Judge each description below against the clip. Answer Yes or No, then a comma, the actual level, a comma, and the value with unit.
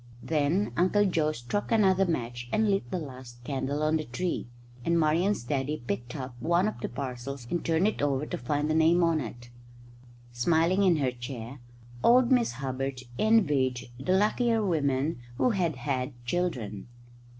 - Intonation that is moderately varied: No, wide, 6.0 semitones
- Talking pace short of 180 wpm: Yes, average, 165 wpm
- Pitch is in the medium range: Yes, medium, 150 Hz